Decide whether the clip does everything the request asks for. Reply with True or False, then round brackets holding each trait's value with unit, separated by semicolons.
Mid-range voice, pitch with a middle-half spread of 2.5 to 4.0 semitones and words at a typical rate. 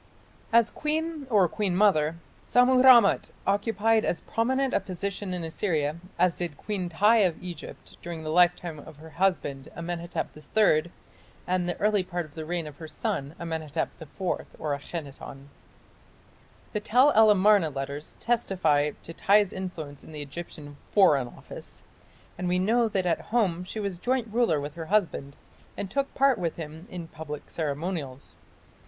False (175 Hz; 5.1 semitones; 160 wpm)